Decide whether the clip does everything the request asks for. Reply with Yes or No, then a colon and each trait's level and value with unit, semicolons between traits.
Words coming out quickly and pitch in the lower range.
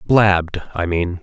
No: average, 145 wpm; very low, 95 Hz